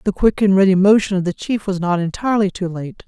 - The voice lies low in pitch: No, high, 190 Hz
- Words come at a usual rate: No, fast, 255 wpm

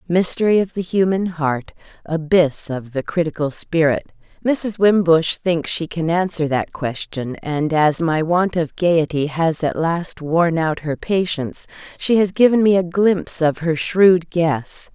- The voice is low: No, medium, 165 Hz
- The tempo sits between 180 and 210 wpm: No, average, 160 wpm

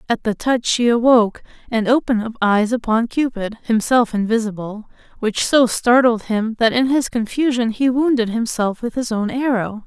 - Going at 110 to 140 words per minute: No, average, 165 wpm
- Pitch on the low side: No, high, 230 Hz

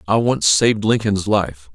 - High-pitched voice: No, low, 100 Hz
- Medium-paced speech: Yes, average, 170 wpm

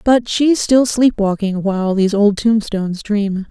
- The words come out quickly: No, average, 170 wpm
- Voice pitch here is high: Yes, high, 210 Hz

